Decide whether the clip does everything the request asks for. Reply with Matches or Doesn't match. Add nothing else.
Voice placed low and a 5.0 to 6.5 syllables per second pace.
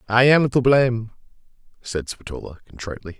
Matches